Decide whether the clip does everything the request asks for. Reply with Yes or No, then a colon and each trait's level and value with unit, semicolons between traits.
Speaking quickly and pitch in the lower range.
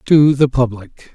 No: average, 155 wpm; low, 130 Hz